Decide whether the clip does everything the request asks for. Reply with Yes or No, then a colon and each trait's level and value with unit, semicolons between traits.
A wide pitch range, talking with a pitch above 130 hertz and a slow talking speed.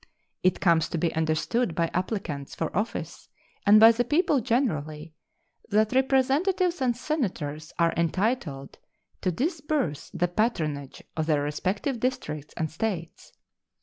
Yes: wide, 8.0 semitones; medium, 185 Hz; slow, 130 wpm